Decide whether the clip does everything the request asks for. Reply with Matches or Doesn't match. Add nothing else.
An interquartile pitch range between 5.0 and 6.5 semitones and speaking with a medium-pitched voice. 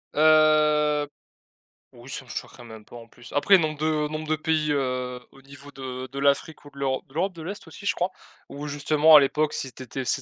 Doesn't match